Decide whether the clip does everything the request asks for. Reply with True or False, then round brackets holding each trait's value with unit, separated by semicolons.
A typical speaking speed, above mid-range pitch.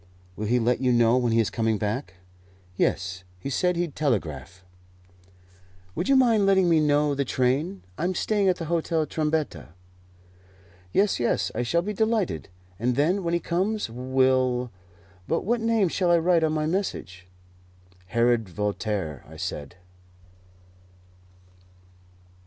False (145 wpm; 140 Hz)